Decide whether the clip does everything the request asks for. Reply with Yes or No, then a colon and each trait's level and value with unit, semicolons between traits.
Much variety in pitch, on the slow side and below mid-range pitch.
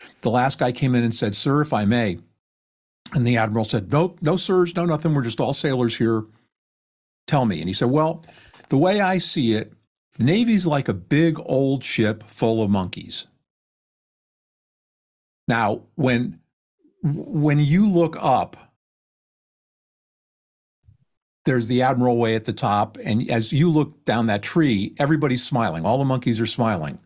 No: wide, 5.8 semitones; average, 160 wpm; low, 125 Hz